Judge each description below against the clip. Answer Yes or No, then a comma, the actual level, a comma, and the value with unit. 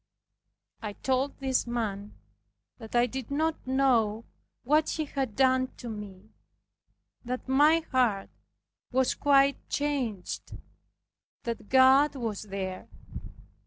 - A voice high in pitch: Yes, very high, 255 Hz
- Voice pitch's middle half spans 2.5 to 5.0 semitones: Yes, average, 3.9 semitones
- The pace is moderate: No, slow, 110 wpm